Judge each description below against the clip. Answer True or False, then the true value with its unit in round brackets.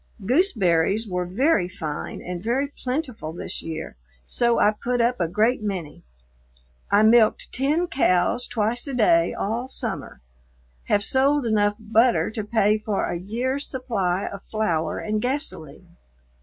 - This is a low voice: False (220 Hz)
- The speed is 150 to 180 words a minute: False (140 wpm)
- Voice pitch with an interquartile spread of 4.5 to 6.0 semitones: True (5.2 semitones)